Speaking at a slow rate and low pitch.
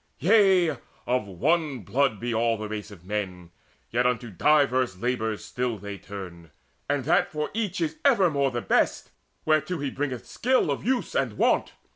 No: average, 165 wpm; low, 125 Hz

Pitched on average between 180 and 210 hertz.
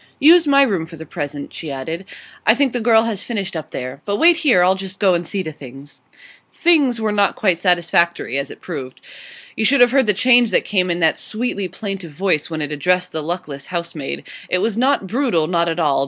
Yes: medium, 185 Hz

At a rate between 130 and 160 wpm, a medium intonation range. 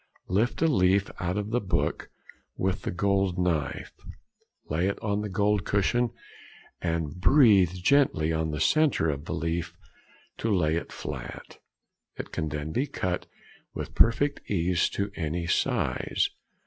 Yes: average, 150 wpm; average, 4.1 semitones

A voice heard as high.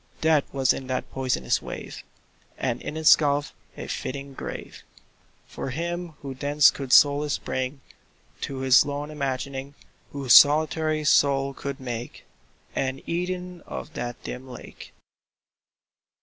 No: medium, 140 Hz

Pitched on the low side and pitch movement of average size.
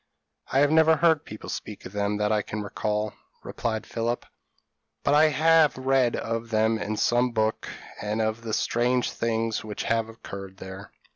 Yes: low, 115 Hz; average, 3.1 semitones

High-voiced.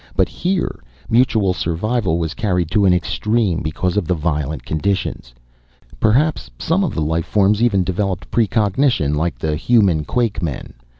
No: very low, 95 Hz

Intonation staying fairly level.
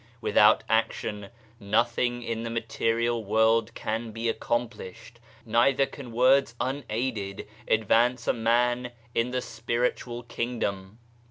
Yes: narrow, 1.5 semitones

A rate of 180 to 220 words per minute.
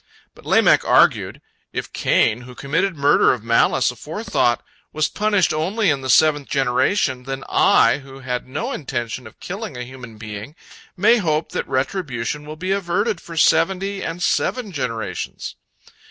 No: average, 155 wpm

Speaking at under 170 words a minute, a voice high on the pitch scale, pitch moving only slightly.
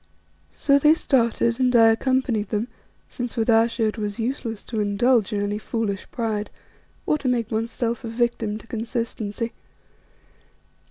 Yes: average, 150 wpm; high, 230 Hz; narrow, 2.1 semitones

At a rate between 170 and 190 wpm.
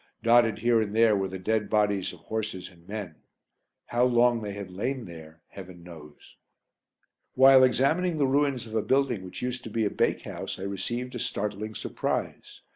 Yes: average, 180 wpm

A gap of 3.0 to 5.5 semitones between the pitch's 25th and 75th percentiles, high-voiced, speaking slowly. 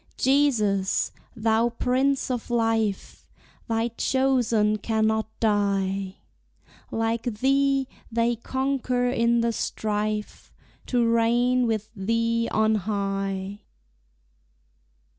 No: narrow, 2.6 semitones; high, 230 Hz; slow, 85 wpm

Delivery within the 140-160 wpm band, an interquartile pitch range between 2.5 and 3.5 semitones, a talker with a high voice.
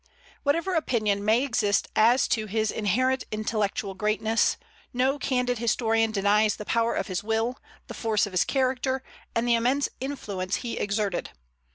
Yes: average, 155 wpm; average, 3.2 semitones; high, 225 Hz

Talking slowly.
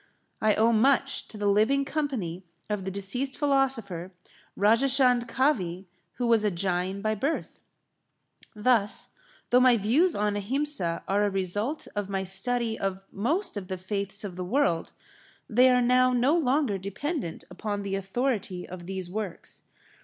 No: average, 155 wpm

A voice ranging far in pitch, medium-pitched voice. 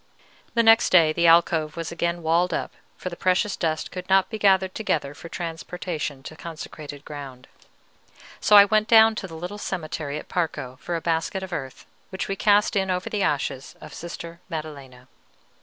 No: average, 3.6 semitones; medium, 170 Hz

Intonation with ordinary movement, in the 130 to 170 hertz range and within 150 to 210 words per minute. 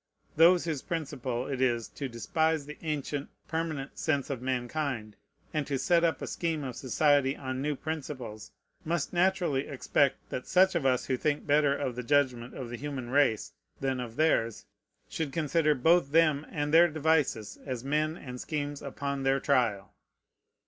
Yes: average, 3.3 semitones; medium, 140 Hz; average, 170 wpm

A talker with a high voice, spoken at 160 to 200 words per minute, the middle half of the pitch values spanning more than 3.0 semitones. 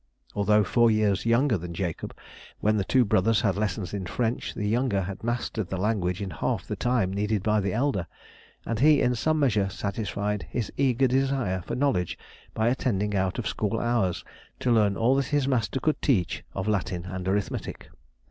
No: low, 105 Hz; average, 185 wpm; average, 4.0 semitones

